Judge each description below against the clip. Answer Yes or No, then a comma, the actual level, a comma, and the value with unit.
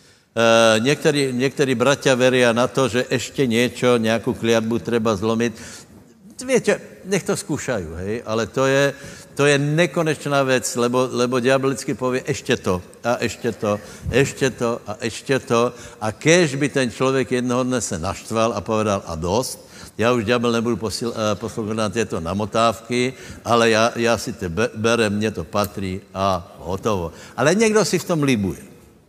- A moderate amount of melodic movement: Yes, average, 3.2 semitones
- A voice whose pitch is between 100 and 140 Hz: Yes, low, 120 Hz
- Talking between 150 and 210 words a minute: Yes, average, 160 wpm